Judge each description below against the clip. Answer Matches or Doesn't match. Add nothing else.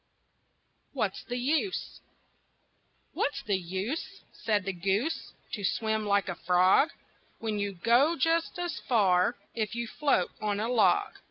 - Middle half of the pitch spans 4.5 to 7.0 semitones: Matches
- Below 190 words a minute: Matches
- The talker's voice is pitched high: Matches